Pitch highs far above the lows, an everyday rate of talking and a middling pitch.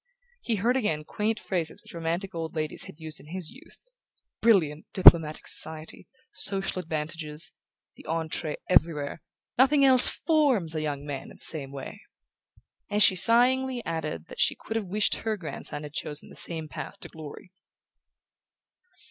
Yes: wide, 5.7 semitones; average, 155 wpm; medium, 165 Hz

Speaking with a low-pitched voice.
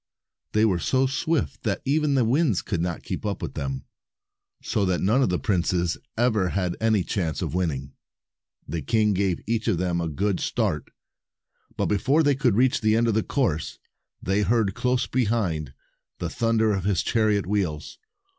Yes: low, 105 Hz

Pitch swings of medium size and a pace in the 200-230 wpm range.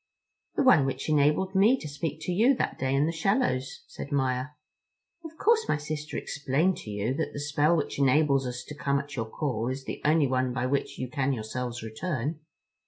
Yes: average, 3.6 semitones; fast, 205 wpm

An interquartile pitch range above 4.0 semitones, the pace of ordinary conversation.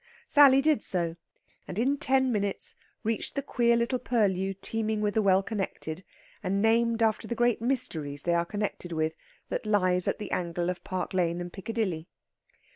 Yes: average, 4.6 semitones; average, 175 wpm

